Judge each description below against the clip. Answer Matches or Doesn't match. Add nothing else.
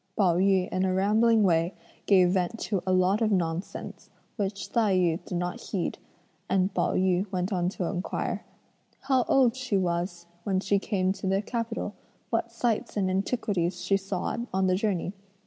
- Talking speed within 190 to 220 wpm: Doesn't match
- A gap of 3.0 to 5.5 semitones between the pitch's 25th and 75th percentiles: Doesn't match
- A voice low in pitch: Doesn't match